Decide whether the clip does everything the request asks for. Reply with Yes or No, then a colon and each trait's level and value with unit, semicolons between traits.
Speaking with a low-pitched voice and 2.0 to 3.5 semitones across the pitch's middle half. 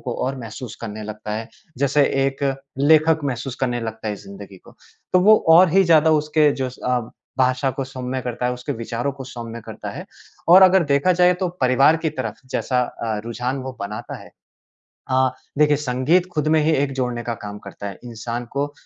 No: low, 130 Hz; average, 4.2 semitones